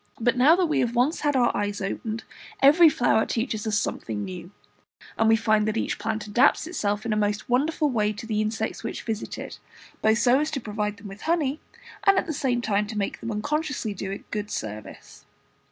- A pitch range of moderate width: Yes, average, 4.2 semitones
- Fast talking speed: Yes, fast, 215 wpm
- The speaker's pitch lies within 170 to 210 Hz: No, high, 225 Hz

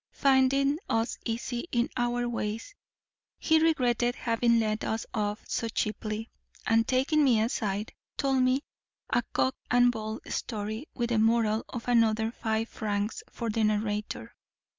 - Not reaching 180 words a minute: Yes, average, 140 wpm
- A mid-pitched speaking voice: No, high, 230 Hz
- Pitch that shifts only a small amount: Yes, narrow, 2.3 semitones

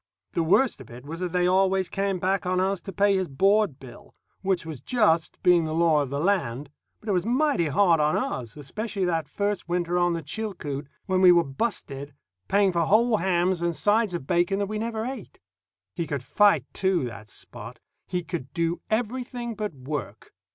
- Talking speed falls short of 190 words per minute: No, average, 200 wpm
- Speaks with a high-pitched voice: No, medium, 180 Hz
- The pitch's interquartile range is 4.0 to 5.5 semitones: Yes, average, 4.6 semitones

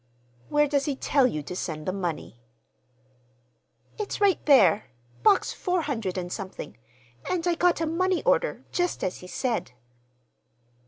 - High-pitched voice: Yes, very high, 270 Hz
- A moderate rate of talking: Yes, average, 145 wpm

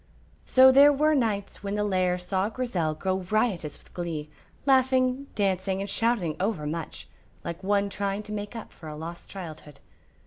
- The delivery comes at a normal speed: Yes, average, 170 wpm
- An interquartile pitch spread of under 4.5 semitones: No, average, 4.8 semitones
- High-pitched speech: Yes, high, 200 Hz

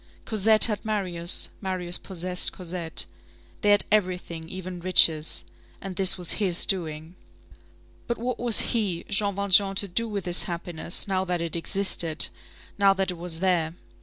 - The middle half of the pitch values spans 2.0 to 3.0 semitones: Yes, average, 2.7 semitones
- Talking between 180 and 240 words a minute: No, average, 155 wpm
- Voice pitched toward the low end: No, medium, 185 Hz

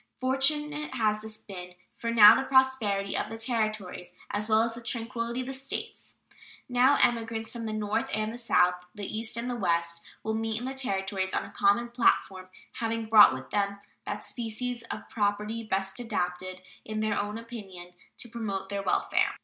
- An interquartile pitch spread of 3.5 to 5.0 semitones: No, average, 3.0 semitones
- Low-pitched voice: No, high, 220 Hz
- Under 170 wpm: No, average, 180 wpm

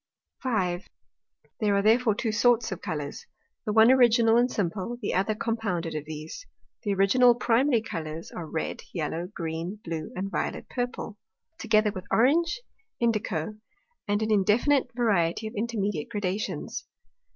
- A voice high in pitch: Yes, high, 210 Hz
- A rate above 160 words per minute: No, average, 150 wpm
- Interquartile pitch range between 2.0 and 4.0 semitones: No, average, 4.8 semitones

